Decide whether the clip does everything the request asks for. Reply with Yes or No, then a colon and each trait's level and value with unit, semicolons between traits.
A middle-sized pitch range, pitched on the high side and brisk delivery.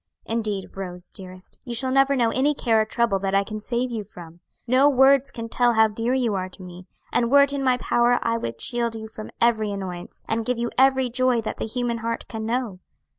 Yes: average, 3.3 semitones; high, 230 Hz; fast, 230 wpm